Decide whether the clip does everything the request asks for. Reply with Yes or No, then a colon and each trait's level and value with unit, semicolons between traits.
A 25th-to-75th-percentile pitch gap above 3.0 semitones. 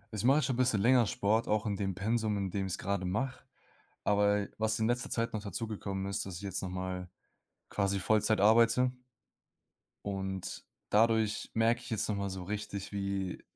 No: narrow, 2.5 semitones